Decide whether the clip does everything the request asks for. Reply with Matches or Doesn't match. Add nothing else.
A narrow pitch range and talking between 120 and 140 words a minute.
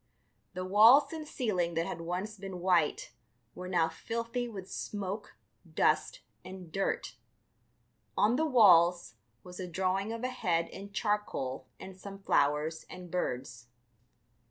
Doesn't match